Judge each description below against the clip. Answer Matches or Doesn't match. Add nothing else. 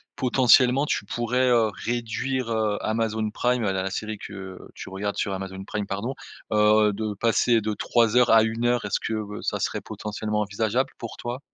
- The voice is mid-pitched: Doesn't match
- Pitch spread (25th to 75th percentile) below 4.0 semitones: Matches